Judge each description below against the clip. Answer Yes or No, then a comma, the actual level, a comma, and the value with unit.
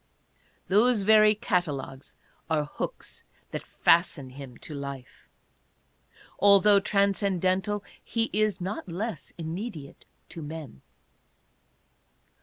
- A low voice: No, medium, 185 Hz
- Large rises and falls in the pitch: Yes, wide, 5.7 semitones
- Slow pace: Yes, slow, 100 wpm